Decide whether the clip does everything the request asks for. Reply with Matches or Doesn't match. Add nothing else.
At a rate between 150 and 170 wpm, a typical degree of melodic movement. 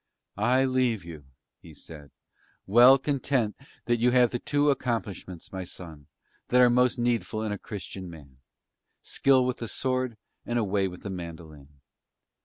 Doesn't match